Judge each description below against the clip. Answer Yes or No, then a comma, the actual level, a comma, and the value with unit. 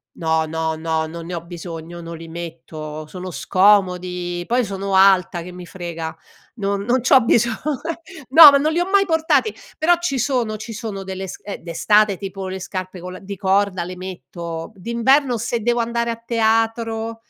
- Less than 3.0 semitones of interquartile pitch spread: No, average, 5.2 semitones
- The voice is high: Yes, high, 195 Hz